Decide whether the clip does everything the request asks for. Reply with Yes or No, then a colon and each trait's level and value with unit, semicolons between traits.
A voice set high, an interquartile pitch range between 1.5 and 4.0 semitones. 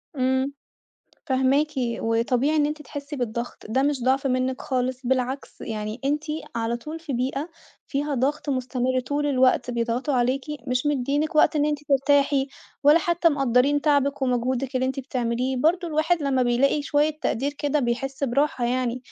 Yes: very high, 265 Hz; narrow, 2.6 semitones